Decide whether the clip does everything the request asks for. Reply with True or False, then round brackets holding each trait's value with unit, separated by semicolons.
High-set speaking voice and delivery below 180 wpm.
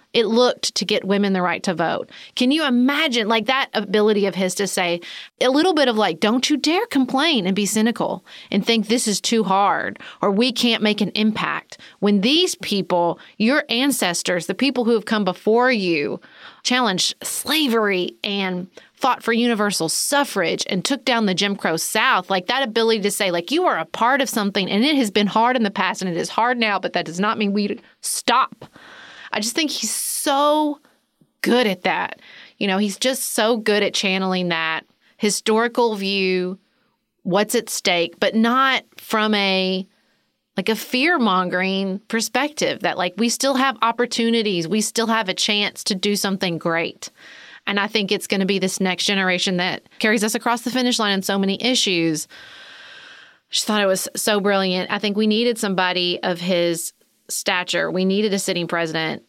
False (215 Hz; 190 wpm)